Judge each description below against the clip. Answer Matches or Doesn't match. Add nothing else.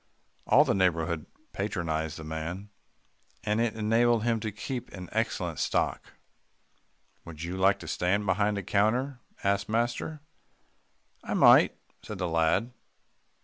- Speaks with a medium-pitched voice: Doesn't match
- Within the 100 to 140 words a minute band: Matches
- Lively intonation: Doesn't match